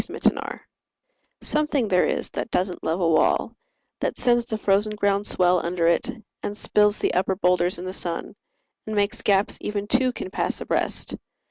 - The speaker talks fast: No, average, 175 wpm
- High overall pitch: Yes, high, 200 Hz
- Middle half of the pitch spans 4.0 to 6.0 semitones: No, average, 2.9 semitones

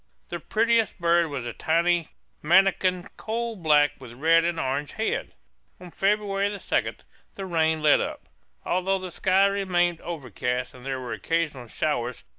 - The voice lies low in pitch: No, medium, 170 Hz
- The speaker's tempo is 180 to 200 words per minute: No, average, 155 wpm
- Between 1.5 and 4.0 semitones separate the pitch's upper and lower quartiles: No, average, 4.7 semitones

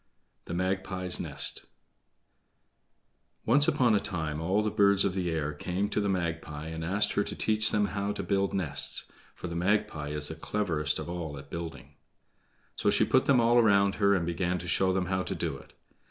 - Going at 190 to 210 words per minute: Yes, average, 195 wpm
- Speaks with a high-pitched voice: No, very low, 90 Hz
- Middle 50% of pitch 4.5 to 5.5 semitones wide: No, average, 3.8 semitones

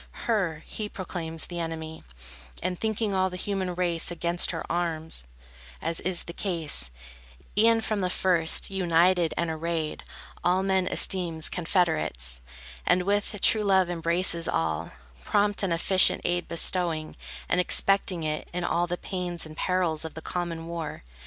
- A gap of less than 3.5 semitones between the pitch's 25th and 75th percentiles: Yes, narrow, 2.4 semitones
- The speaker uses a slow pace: No, average, 150 wpm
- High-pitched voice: No, medium, 175 Hz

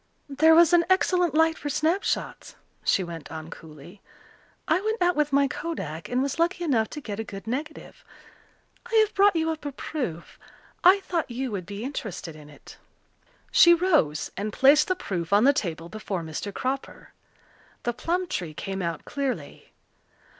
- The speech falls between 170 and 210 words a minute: Yes, average, 175 wpm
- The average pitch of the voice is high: Yes, very high, 270 Hz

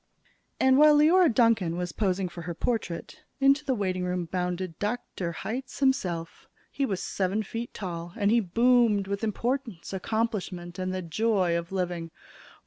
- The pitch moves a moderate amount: Yes, average, 5.0 semitones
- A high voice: Yes, high, 195 Hz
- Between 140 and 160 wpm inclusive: Yes, average, 150 wpm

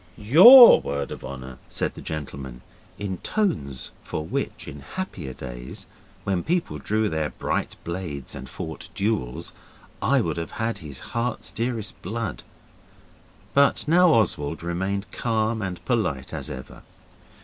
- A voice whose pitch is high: No, very low, 95 Hz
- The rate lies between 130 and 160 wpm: Yes, average, 140 wpm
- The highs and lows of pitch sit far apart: Yes, wide, 8.3 semitones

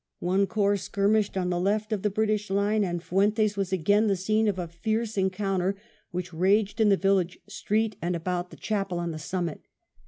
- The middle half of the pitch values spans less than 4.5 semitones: Yes, average, 2.7 semitones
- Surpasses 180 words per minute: Yes, average, 195 wpm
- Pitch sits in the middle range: No, high, 195 Hz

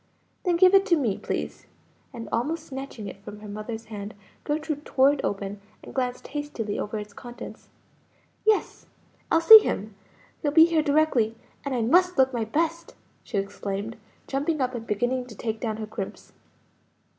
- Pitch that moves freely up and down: Yes, wide, 6.1 semitones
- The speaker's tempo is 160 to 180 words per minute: Yes, average, 170 wpm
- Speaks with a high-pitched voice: Yes, very high, 250 Hz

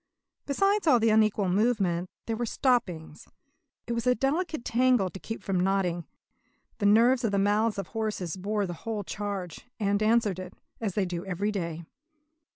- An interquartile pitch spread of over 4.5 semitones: No, average, 3.8 semitones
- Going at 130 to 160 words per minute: No, average, 175 wpm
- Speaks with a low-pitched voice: No, high, 205 Hz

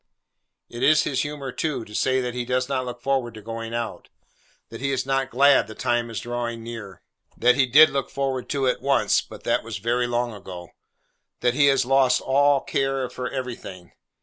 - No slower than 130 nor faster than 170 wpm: No, average, 200 wpm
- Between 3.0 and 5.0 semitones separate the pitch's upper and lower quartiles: No, narrow, 2.4 semitones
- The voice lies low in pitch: Yes, low, 125 Hz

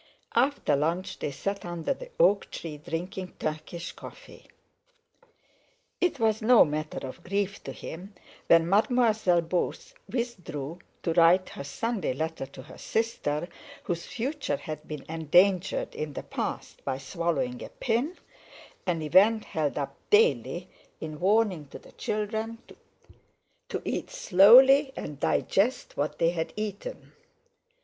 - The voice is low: No, medium, 180 Hz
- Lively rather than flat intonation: Yes, wide, 6.2 semitones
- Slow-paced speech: Yes, slow, 130 wpm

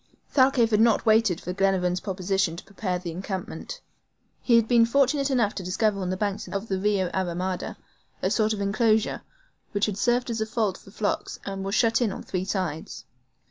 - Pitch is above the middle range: Yes, high, 200 Hz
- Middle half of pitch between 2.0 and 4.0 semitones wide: Yes, average, 3.3 semitones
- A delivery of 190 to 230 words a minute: Yes, average, 200 wpm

